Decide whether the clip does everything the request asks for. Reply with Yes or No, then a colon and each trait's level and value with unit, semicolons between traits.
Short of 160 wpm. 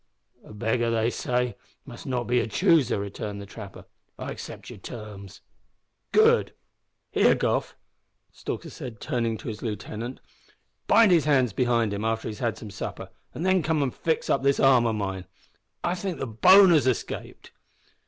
No: average, 170 wpm